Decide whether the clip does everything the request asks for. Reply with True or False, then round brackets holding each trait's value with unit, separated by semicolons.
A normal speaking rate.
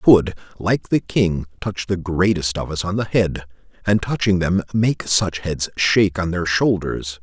True (190 wpm)